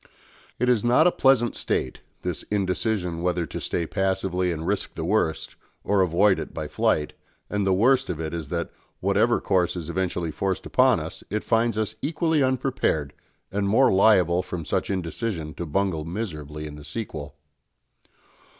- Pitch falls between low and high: No, very low, 95 Hz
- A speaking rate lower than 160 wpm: No, average, 170 wpm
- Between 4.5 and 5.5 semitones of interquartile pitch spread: Yes, average, 5.0 semitones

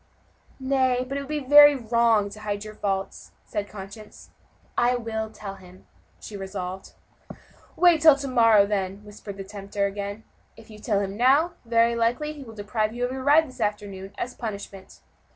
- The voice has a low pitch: No, high, 220 Hz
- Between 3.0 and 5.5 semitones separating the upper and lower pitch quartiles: Yes, average, 4.1 semitones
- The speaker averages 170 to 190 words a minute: Yes, average, 180 wpm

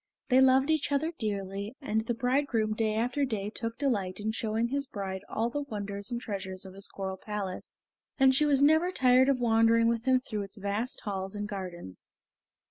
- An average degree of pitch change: Yes, average, 4.5 semitones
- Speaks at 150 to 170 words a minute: No, average, 195 wpm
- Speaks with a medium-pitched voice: No, high, 225 Hz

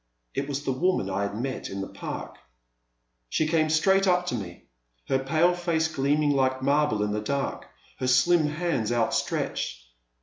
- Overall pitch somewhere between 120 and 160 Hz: Yes, medium, 140 Hz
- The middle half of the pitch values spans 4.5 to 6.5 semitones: Yes, average, 5.2 semitones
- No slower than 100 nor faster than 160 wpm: No, average, 170 wpm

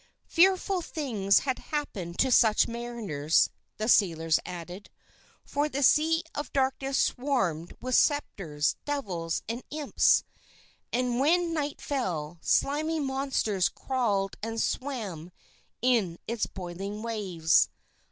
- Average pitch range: No, wide, 7.6 semitones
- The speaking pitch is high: Yes, high, 235 Hz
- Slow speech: Yes, slow, 115 wpm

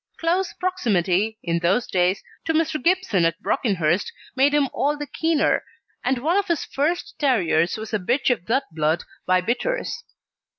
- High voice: Yes, high, 245 Hz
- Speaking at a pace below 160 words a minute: No, average, 165 wpm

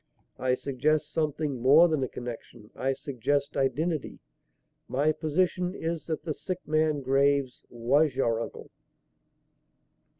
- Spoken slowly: Yes, slow, 125 wpm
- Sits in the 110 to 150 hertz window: Yes, medium, 140 Hz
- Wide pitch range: No, average, 3.2 semitones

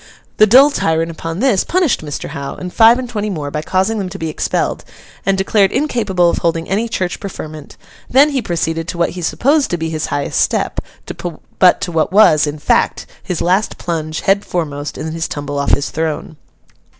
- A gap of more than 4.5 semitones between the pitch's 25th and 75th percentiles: Yes, average, 5.0 semitones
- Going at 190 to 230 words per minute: Yes, average, 200 wpm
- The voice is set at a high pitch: No, medium, 175 Hz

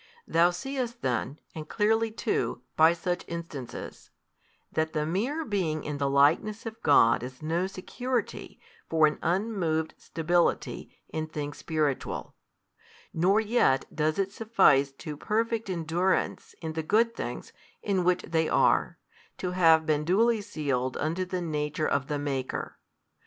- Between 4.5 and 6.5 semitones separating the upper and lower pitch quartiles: Yes, average, 5.0 semitones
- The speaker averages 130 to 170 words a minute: Yes, average, 140 wpm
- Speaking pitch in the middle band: Yes, medium, 165 Hz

